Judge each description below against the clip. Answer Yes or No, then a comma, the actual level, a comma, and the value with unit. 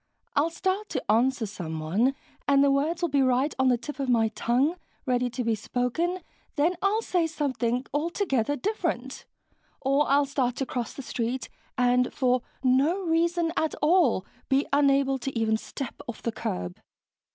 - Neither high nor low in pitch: No, very high, 270 Hz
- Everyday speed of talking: Yes, average, 165 wpm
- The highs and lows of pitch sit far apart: No, average, 4.2 semitones